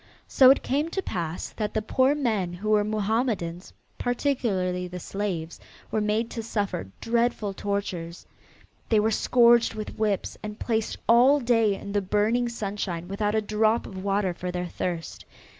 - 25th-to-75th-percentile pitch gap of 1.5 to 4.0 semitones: Yes, average, 3.7 semitones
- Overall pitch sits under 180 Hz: No, high, 210 Hz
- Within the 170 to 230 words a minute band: No, average, 160 wpm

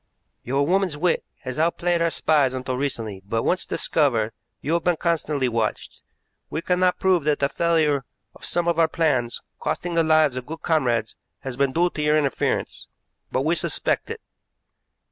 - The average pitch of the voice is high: No, medium, 150 Hz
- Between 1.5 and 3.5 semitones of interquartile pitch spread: No, average, 4.5 semitones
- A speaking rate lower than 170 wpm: No, average, 175 wpm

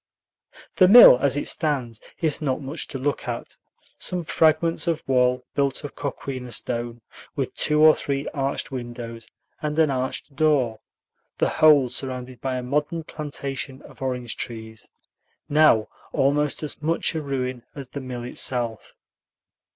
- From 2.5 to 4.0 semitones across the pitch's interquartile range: Yes, average, 3.3 semitones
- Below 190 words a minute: Yes, average, 150 wpm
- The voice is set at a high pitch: No, low, 135 Hz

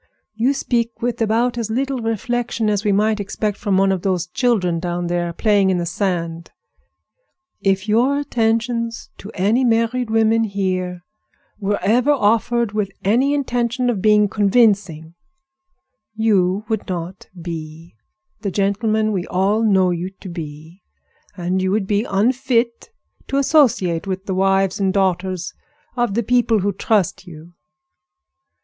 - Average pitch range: Yes, average, 3.8 semitones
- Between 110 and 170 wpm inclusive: Yes, average, 145 wpm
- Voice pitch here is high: Yes, high, 205 Hz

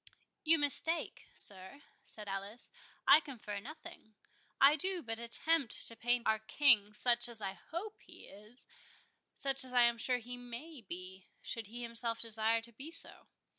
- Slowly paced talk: No, average, 160 wpm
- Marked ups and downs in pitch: No, average, 4.3 semitones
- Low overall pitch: No, high, 235 Hz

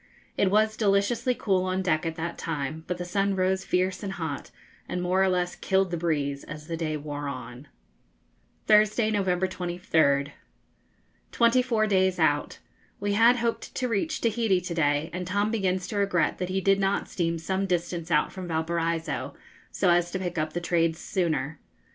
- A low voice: No, medium, 180 Hz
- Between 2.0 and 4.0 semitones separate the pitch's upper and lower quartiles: Yes, average, 3.3 semitones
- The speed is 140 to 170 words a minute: No, average, 180 wpm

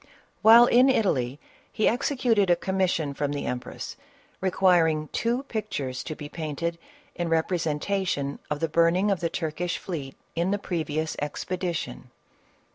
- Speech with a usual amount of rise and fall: Yes, average, 4.3 semitones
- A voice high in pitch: No, medium, 170 Hz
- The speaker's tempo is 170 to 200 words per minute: No, slow, 135 wpm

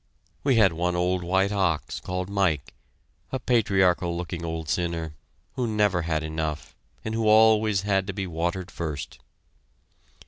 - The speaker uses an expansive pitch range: No, average, 3.5 semitones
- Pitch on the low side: Yes, very low, 90 Hz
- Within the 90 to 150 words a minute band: Yes, average, 145 wpm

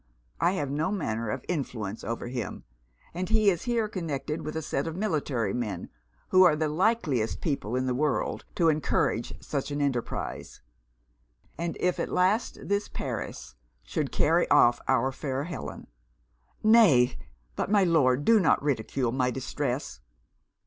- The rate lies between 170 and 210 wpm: No, average, 155 wpm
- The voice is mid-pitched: Yes, medium, 145 Hz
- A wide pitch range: Yes, wide, 6.2 semitones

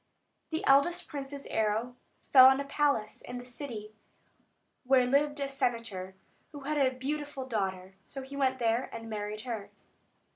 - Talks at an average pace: Yes, average, 155 wpm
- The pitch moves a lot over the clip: No, average, 4.0 semitones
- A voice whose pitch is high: Yes, very high, 260 Hz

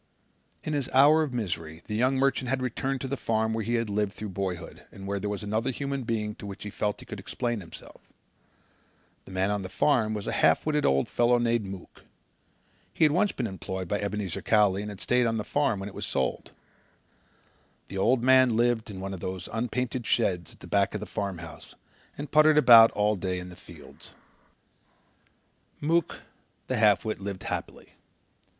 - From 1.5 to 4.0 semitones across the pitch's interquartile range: No, average, 4.4 semitones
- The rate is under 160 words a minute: No, average, 195 wpm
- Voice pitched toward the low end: Yes, low, 110 Hz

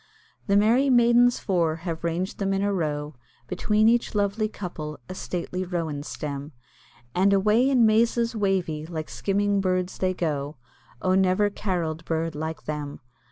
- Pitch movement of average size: Yes, average, 4.4 semitones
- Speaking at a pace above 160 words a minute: No, average, 155 wpm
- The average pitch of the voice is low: No, medium, 185 Hz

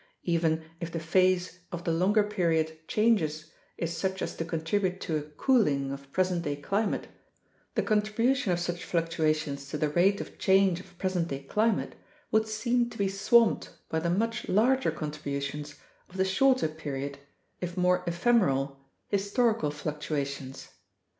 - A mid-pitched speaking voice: Yes, medium, 175 Hz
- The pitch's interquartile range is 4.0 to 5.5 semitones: Yes, average, 4.8 semitones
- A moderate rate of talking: Yes, average, 155 wpm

